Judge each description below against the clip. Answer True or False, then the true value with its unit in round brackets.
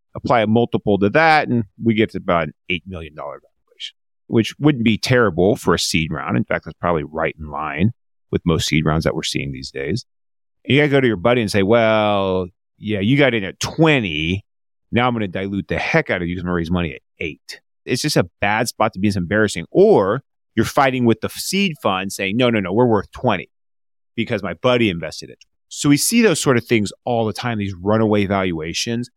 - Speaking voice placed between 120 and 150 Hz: False (105 Hz)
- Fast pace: True (230 wpm)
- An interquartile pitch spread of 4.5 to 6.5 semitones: True (4.9 semitones)